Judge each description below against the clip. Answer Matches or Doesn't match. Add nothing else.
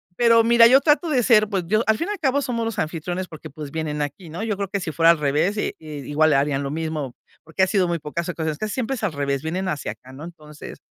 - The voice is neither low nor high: Matches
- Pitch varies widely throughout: Matches